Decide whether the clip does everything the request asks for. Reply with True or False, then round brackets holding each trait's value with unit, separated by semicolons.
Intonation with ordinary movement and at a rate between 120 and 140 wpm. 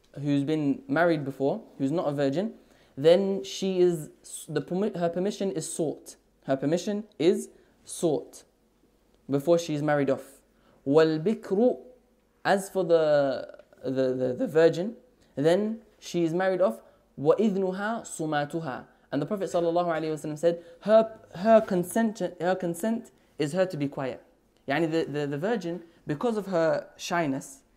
True (5.0 semitones; 135 wpm)